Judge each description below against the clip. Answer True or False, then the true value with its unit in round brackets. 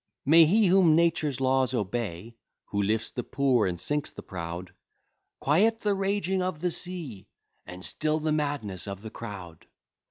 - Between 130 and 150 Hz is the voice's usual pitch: True (135 Hz)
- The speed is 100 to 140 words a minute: False (160 wpm)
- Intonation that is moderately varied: False (8.6 semitones)